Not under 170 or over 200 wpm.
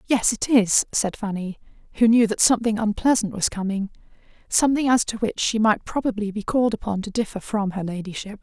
Yes: average, 185 wpm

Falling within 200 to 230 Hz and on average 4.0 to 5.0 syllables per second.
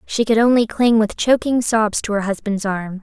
Yes: high, 220 Hz; 4.8 syllables/s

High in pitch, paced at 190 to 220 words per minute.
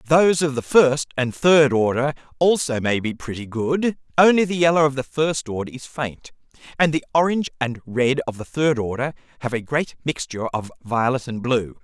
No: low, 135 Hz; average, 195 wpm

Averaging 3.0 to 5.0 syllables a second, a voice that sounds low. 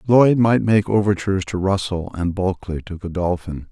No: 5.2 syllables/s; very low, 95 Hz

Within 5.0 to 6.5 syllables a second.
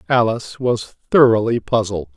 No: 4.6 syllables/s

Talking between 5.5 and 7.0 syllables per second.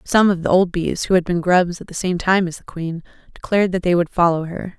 Yes: 5.7 syllables/s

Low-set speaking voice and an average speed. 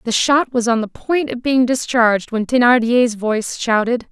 No: high, 240 Hz; average, 190 wpm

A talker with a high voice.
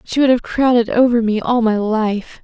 Yes: high, 230 Hz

